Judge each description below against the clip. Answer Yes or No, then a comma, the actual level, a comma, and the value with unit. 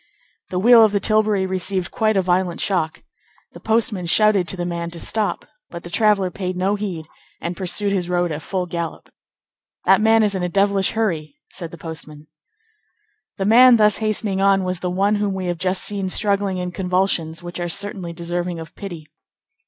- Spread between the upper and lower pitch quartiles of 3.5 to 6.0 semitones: No, average, 2.7 semitones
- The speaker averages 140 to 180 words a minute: No, average, 190 wpm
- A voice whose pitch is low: No, medium, 185 Hz